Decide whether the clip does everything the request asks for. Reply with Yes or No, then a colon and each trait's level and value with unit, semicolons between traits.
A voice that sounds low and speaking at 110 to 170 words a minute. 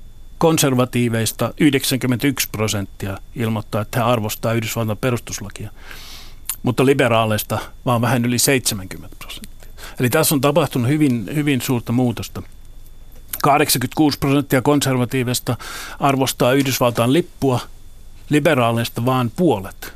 No: low, 125 Hz; average, 100 wpm